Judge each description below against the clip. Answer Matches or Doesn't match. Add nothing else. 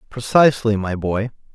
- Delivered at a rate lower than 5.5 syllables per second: Matches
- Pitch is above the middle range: Doesn't match